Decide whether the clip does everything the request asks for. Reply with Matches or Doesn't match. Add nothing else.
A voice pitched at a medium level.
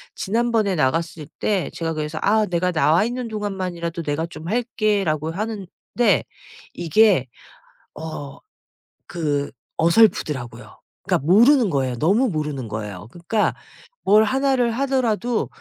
Matches